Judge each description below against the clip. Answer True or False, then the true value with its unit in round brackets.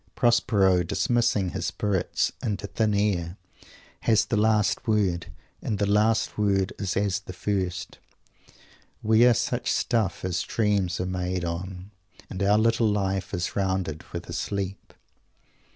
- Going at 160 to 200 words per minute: False (140 wpm)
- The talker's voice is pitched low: True (100 Hz)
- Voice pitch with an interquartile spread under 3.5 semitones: True (2.5 semitones)